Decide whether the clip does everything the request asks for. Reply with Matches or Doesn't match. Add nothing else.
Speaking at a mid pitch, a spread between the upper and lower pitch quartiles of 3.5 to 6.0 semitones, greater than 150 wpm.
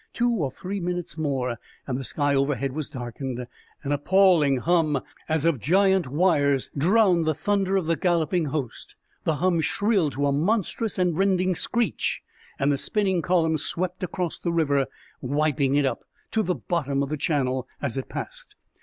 Matches